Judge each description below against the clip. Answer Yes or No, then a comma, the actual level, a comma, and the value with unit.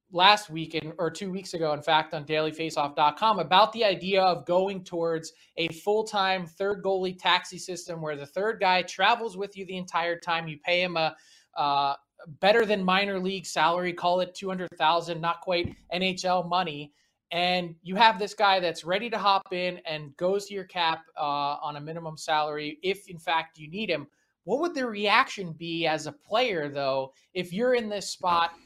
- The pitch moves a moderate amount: Yes, average, 3.2 semitones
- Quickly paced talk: No, average, 185 wpm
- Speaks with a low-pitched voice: No, medium, 175 Hz